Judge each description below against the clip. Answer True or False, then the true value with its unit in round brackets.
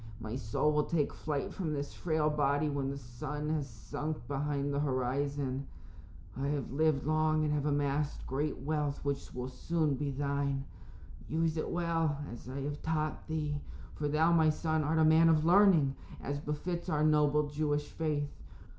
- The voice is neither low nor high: True (150 Hz)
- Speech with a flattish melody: True (1.8 semitones)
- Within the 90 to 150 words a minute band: False (170 wpm)